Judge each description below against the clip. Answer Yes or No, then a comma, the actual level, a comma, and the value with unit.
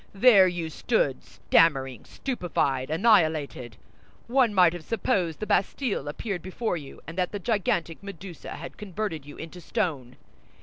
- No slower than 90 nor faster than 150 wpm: Yes, average, 140 wpm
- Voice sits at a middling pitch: Yes, medium, 175 Hz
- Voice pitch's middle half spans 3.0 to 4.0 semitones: No, average, 4.9 semitones